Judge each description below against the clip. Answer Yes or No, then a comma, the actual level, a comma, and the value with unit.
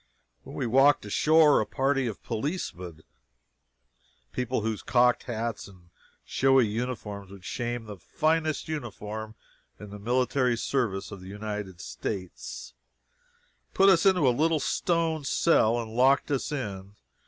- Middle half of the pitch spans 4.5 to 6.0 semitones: Yes, average, 5.3 semitones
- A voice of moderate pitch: No, low, 120 Hz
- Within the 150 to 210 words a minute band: No, slow, 135 wpm